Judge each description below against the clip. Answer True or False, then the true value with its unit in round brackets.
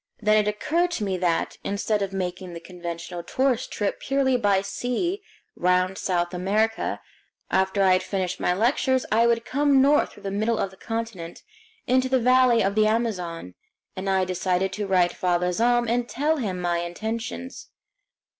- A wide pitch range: False (4.6 semitones)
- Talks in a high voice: True (205 Hz)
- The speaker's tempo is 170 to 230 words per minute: True (175 wpm)